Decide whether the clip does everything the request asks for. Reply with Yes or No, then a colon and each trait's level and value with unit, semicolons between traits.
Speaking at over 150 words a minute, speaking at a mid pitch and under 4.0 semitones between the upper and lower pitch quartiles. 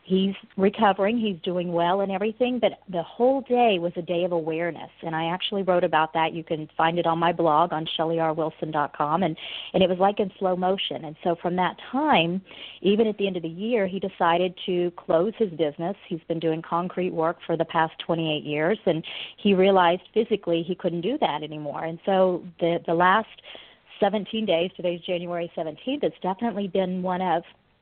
Yes: average, 195 wpm; medium, 180 Hz; average, 2.9 semitones